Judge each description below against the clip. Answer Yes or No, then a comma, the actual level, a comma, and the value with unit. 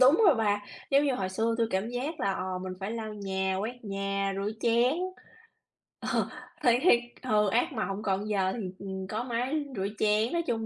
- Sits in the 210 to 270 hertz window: Yes, high, 215 Hz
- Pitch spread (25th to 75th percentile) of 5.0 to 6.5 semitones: No, average, 3.8 semitones